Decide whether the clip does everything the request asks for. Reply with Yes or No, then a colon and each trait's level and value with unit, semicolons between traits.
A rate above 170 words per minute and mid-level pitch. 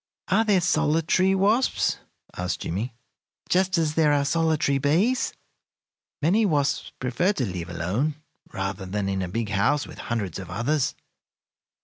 No: average, 140 wpm; medium, 145 Hz